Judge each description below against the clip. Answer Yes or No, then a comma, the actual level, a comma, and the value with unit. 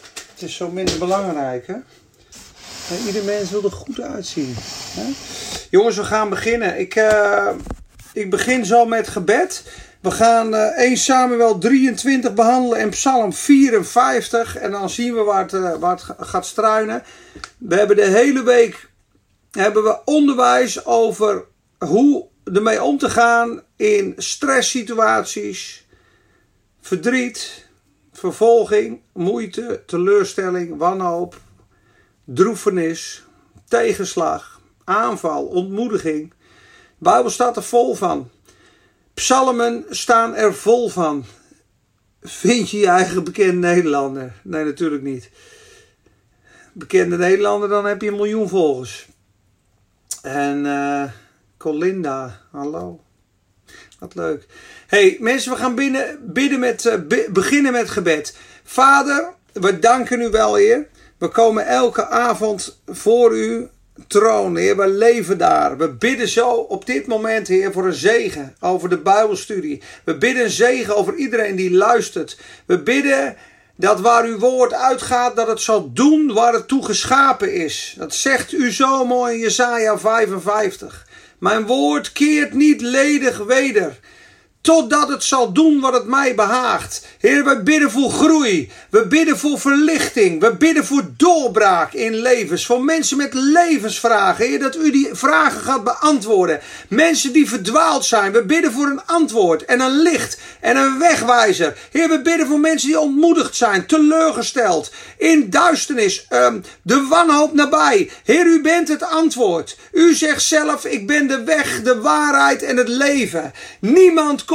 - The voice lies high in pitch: Yes, high, 235 Hz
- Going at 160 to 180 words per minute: No, average, 140 wpm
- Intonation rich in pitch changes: Yes, wide, 6.5 semitones